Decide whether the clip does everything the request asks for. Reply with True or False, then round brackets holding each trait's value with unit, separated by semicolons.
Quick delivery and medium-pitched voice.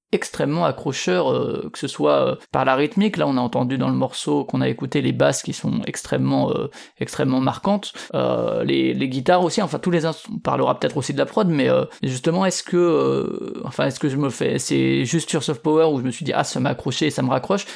True (250 wpm; 145 Hz)